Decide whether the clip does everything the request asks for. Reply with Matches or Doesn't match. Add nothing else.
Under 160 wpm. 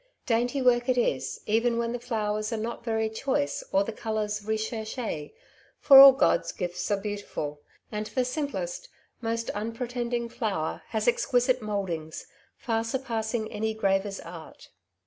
Matches